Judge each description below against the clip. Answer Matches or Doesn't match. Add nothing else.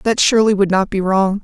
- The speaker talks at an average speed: Doesn't match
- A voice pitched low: Doesn't match